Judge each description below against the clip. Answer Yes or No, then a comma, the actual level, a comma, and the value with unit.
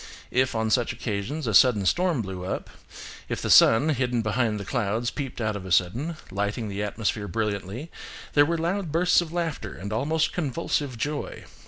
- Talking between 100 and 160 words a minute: No, average, 180 wpm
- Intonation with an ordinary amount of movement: No, wide, 6.6 semitones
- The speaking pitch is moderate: No, low, 120 Hz